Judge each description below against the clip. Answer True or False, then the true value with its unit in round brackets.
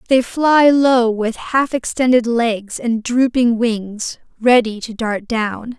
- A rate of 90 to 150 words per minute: True (145 wpm)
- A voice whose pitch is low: False (235 Hz)